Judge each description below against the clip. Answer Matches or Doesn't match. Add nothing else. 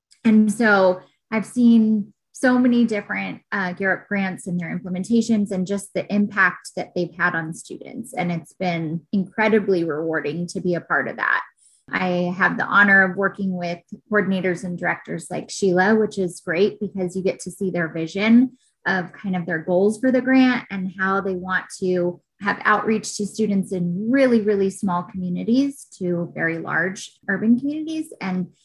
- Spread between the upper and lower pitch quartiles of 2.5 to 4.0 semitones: Matches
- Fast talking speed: Doesn't match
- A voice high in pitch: Matches